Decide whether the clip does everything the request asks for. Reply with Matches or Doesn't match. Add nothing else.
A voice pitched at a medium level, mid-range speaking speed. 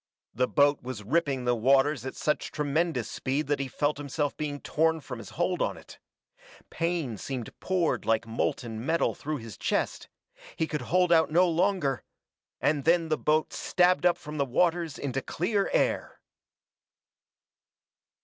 Matches